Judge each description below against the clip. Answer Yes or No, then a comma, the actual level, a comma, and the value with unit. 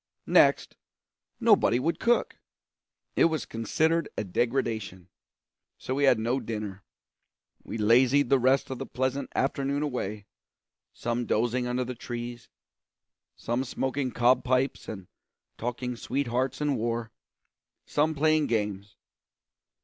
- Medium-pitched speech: No, low, 125 Hz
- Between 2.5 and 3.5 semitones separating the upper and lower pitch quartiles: Yes, average, 2.9 semitones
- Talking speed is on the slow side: Yes, slow, 120 wpm